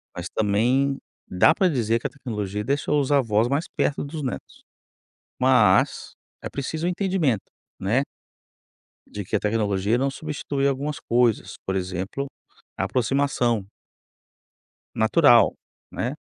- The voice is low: Yes, low, 125 Hz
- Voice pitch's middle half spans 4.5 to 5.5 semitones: Yes, average, 5.1 semitones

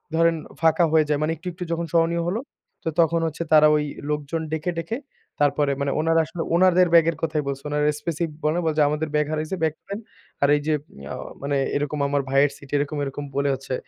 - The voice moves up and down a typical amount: No, narrow, 2.3 semitones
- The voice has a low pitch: No, medium, 155 Hz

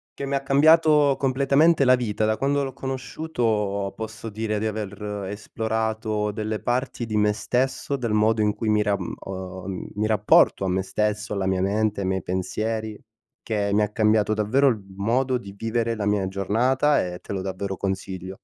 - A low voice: Yes, low, 110 Hz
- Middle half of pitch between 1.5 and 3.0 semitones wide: No, average, 3.6 semitones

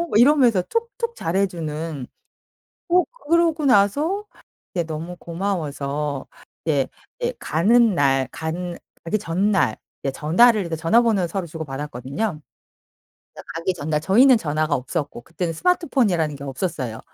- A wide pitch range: Yes, wide, 6.8 semitones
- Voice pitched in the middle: Yes, medium, 170 Hz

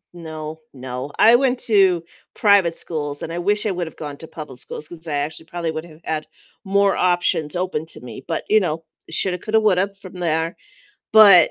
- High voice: No, medium, 170 Hz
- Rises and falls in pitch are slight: No, average, 3.8 semitones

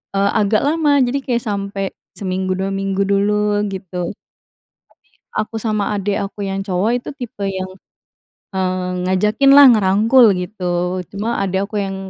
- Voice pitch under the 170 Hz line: No, high, 200 Hz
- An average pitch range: No, narrow, 2.1 semitones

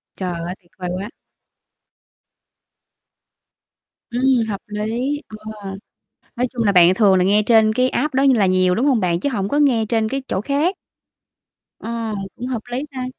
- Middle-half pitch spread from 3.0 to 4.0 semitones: No, average, 4.7 semitones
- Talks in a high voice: Yes, high, 225 Hz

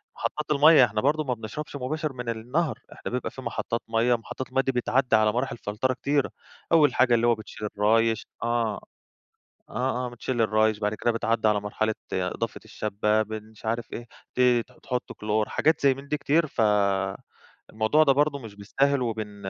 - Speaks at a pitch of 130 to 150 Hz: No, low, 120 Hz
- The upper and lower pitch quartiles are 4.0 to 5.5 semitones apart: No, average, 3.6 semitones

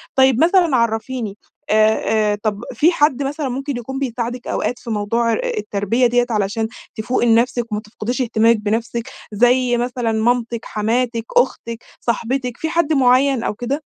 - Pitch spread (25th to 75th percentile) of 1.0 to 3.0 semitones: Yes, narrow, 2.6 semitones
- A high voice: Yes, high, 240 Hz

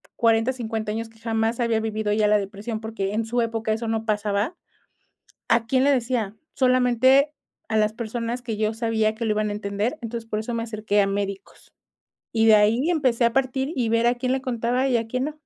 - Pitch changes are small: Yes, narrow, 2.2 semitones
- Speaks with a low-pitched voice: No, high, 225 Hz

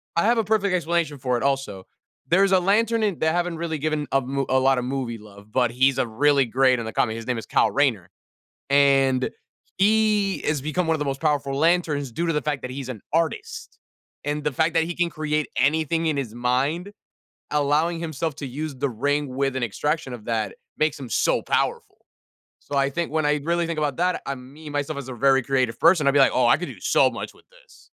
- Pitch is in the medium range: Yes, medium, 145 Hz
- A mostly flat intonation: No, average, 4.0 semitones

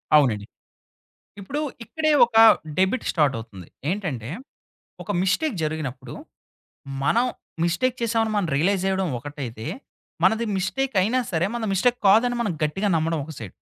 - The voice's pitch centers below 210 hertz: Yes, high, 190 Hz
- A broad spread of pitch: Yes, wide, 7.5 semitones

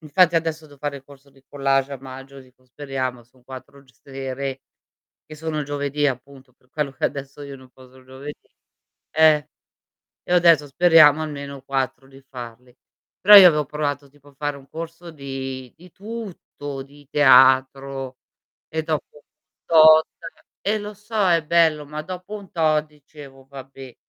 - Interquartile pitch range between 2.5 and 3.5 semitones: Yes, average, 2.8 semitones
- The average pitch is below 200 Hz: Yes, medium, 140 Hz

